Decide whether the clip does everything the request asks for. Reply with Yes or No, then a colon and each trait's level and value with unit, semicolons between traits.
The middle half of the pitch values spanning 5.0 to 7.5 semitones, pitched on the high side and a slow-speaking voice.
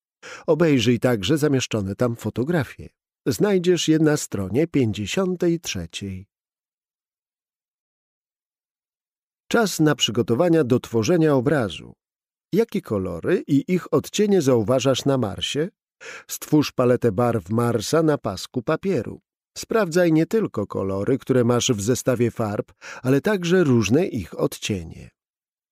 No: wide, 5.6 semitones; low, 130 Hz; slow, 105 wpm